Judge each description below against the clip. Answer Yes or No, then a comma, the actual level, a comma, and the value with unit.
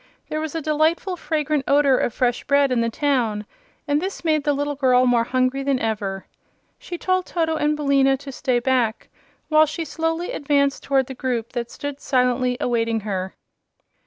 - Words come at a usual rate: Yes, average, 180 wpm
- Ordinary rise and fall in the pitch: Yes, average, 3.6 semitones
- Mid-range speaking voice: No, very high, 275 Hz